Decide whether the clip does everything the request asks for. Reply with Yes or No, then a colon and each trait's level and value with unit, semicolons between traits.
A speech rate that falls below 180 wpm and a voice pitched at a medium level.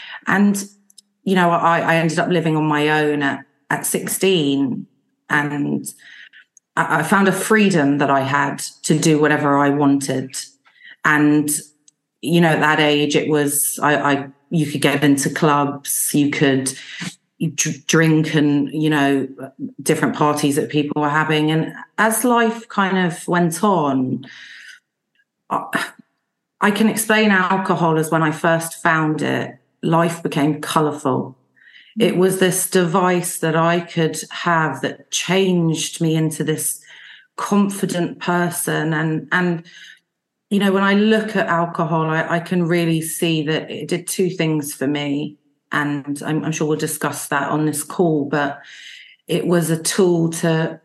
Yes: average, 150 wpm; medium, 160 Hz